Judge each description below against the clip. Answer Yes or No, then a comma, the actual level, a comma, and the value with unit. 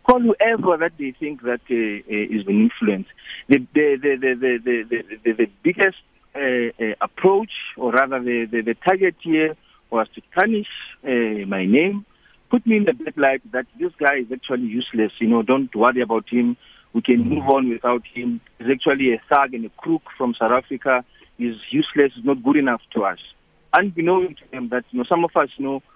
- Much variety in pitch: Yes, wide, 6.8 semitones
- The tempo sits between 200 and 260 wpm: Yes, fast, 205 wpm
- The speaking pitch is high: No, low, 135 Hz